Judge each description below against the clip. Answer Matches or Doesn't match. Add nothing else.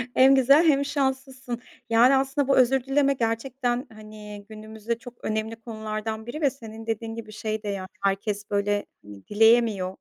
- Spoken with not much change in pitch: Doesn't match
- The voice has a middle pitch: Doesn't match